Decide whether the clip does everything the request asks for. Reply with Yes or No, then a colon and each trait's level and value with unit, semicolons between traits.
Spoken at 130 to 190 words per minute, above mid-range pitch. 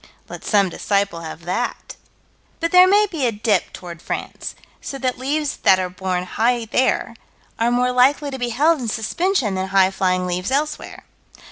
Yes: average, 170 wpm; high, 230 Hz